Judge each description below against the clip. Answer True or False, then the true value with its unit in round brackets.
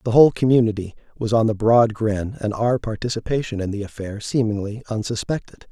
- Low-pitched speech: True (110 Hz)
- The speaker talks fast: False (170 wpm)